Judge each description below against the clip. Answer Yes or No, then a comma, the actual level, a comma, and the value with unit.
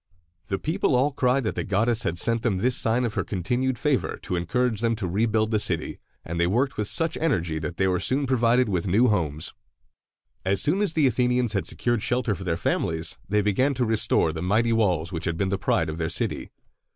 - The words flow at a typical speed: No, fast, 225 wpm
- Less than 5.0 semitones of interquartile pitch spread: No, wide, 5.5 semitones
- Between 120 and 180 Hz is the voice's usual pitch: No, low, 110 Hz